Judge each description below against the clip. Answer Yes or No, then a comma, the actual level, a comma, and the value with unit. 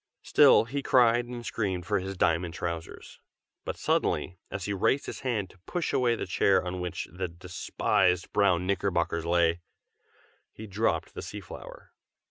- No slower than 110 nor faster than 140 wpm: No, average, 160 wpm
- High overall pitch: No, very low, 95 Hz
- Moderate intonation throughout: Yes, average, 4.0 semitones